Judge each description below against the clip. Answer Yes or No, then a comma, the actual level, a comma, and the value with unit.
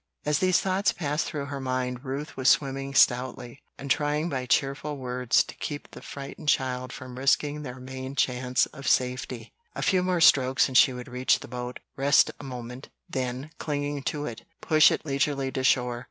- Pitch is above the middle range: No, low, 135 Hz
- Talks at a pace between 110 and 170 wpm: No, average, 185 wpm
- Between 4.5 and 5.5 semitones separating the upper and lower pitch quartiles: No, narrow, 2.4 semitones